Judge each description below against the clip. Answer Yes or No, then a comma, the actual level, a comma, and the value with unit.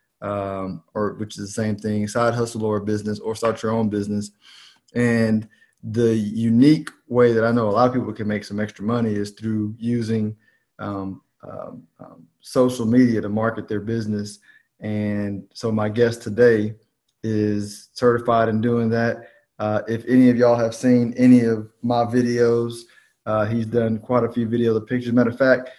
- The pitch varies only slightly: Yes, narrow, 2.1 semitones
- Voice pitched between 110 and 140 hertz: Yes, low, 115 Hz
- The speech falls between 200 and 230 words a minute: No, average, 180 wpm